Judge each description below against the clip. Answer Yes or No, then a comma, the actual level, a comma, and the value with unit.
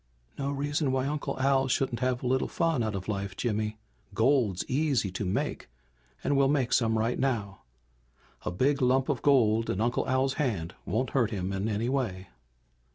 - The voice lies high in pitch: No, low, 125 Hz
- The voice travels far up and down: No, average, 4.2 semitones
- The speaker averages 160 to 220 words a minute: Yes, average, 180 wpm